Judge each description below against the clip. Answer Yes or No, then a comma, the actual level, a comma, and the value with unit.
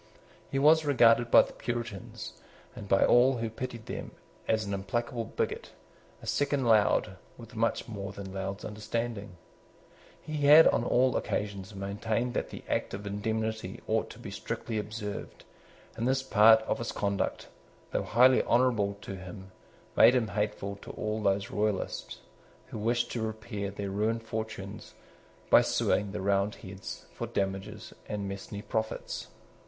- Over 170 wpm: No, average, 150 wpm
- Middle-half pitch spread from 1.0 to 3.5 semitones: Yes, average, 2.8 semitones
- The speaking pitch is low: Yes, low, 110 Hz